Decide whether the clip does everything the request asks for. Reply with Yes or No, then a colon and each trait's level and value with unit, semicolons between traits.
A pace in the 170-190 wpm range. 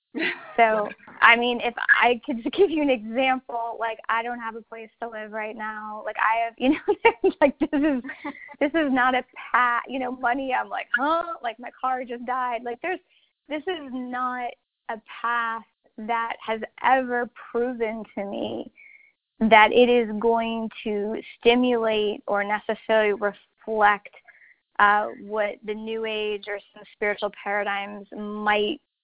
No: average, 160 wpm